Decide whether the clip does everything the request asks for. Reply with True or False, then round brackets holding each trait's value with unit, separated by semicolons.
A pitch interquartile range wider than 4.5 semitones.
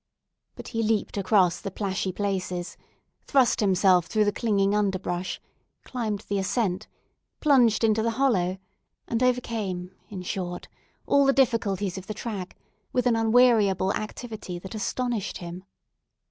False (3.6 semitones)